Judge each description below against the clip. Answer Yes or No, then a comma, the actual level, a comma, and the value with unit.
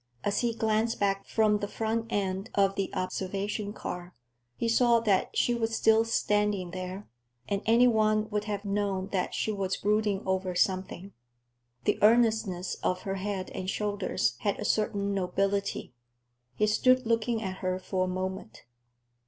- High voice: Yes, high, 200 Hz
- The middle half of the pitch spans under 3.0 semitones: Yes, narrow, 2.6 semitones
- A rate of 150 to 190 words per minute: Yes, average, 160 wpm